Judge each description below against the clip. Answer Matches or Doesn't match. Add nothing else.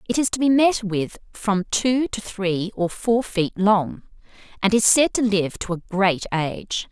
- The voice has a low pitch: Doesn't match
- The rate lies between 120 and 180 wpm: Doesn't match